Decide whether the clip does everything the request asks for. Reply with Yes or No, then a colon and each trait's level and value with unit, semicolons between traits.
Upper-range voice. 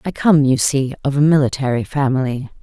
No: medium, 140 Hz